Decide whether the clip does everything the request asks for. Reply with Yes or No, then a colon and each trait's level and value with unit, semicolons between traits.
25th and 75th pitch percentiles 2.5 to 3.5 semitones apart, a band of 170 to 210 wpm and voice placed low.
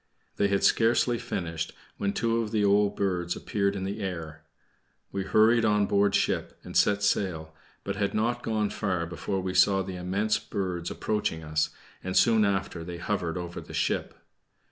Yes: average, 2.9 semitones; average, 175 wpm; low, 100 Hz